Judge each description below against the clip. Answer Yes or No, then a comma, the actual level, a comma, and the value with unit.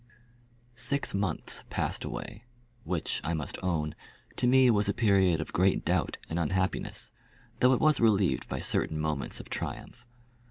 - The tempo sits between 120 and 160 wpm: Yes, average, 155 wpm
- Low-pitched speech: Yes, very low, 95 Hz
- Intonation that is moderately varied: No, wide, 6.3 semitones